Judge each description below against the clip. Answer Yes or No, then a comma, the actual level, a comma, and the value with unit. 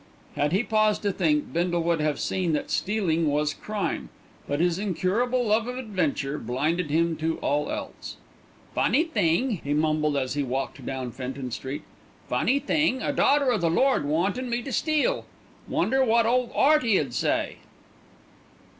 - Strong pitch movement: Yes, wide, 7.9 semitones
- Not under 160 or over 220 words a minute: Yes, average, 165 wpm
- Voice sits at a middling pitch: Yes, medium, 175 Hz